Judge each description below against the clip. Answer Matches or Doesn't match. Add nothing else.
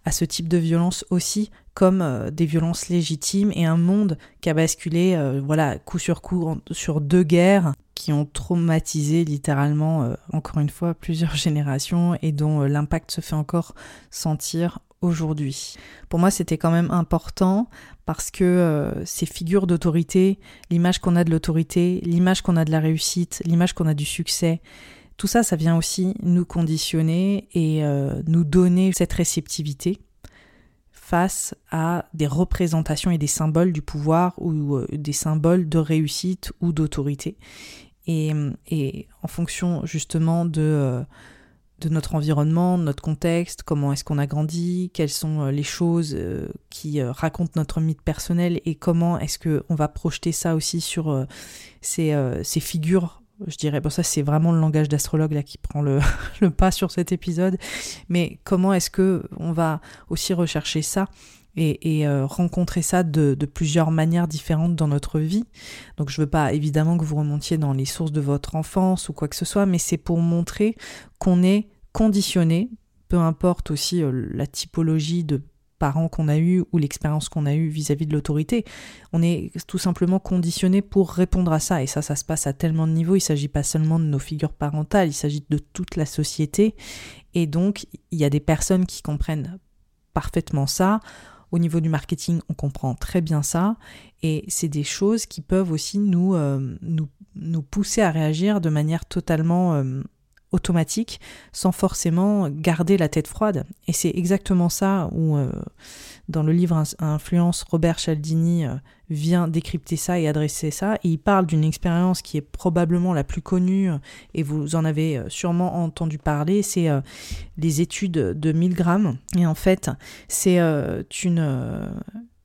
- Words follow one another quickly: Doesn't match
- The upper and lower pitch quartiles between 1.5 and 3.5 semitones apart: Matches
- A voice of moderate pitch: Matches